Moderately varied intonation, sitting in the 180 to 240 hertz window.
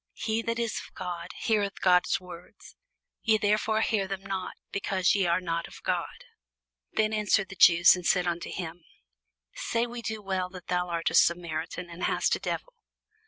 Yes: average, 3.4 semitones; medium, 185 Hz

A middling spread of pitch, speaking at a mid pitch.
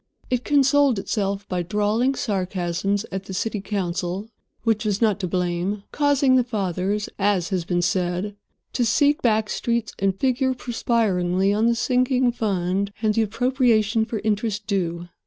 No: average, 3.8 semitones; high, 210 Hz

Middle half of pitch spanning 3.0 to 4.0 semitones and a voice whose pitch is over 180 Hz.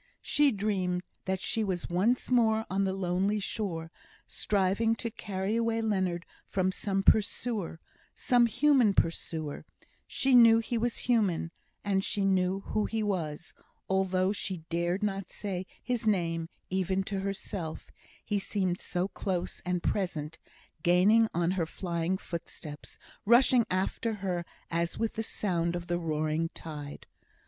Yes: average, 3.7 semitones; high, 190 Hz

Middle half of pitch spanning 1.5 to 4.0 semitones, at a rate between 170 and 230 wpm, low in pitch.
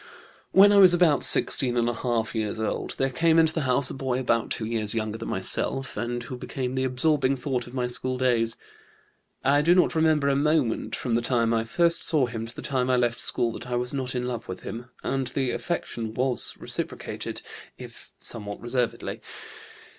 Yes: average, 2.9 semitones; average, 195 wpm; low, 125 Hz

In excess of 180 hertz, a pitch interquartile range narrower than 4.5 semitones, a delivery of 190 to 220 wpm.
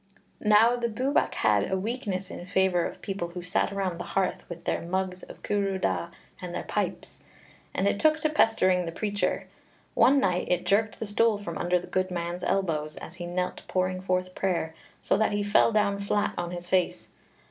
Yes: high, 190 Hz; narrow, 2.5 semitones; average, 200 wpm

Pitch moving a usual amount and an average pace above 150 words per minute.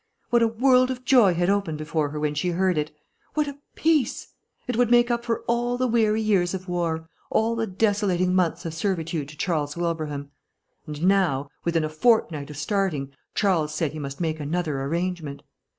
No: wide, 6.3 semitones; average, 190 wpm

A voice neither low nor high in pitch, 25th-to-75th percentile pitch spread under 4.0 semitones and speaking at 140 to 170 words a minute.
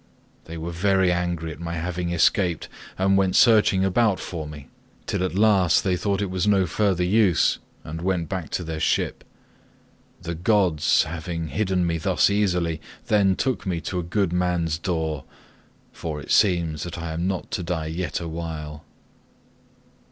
No: very low, 90 Hz; narrow, 2.6 semitones; average, 165 wpm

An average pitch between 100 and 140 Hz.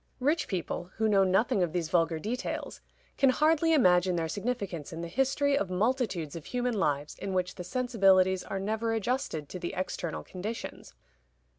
No: high, 195 Hz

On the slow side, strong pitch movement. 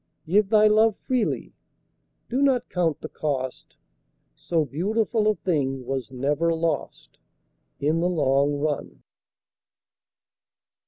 Yes: slow, 110 wpm; wide, 7.0 semitones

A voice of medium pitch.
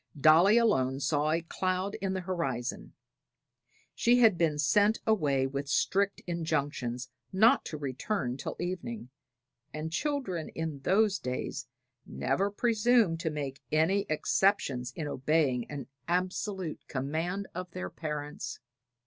Yes: medium, 165 Hz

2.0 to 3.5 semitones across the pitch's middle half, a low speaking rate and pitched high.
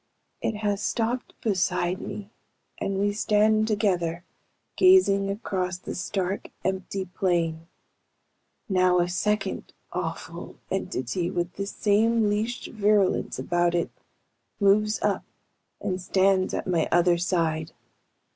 Yes: average, 2.9 semitones; slow, 115 wpm; high, 195 Hz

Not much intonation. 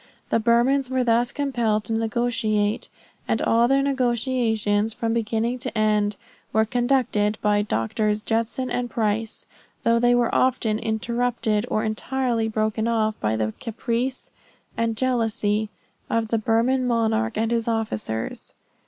Yes: narrow, 2.1 semitones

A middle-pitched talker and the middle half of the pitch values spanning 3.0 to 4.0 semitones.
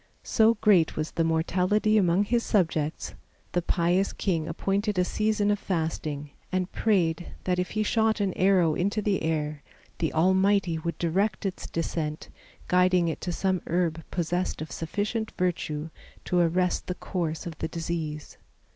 Yes: medium, 180 Hz; average, 3.4 semitones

